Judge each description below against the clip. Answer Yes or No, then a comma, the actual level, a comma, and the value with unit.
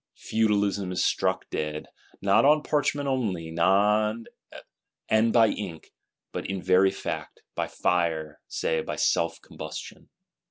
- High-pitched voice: No, very low, 95 Hz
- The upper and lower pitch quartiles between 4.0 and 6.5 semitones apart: Yes, average, 4.7 semitones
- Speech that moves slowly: Yes, slow, 120 wpm